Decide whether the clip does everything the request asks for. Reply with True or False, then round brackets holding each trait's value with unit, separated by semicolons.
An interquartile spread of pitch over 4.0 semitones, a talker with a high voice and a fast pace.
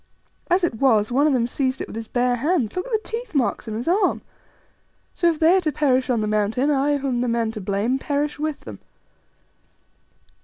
True (4.8 semitones; 265 Hz; 225 wpm)